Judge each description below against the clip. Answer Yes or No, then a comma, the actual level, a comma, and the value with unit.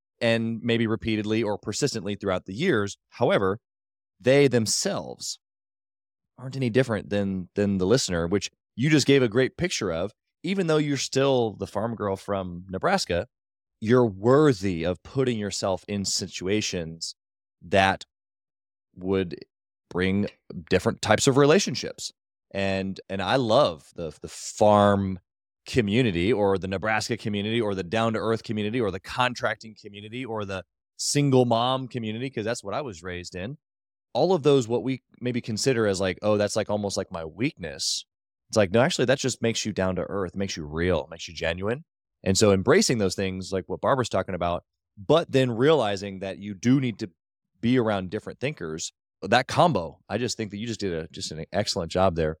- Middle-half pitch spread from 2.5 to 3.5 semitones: No, average, 4.1 semitones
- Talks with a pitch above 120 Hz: No, low, 105 Hz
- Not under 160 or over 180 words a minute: Yes, average, 175 wpm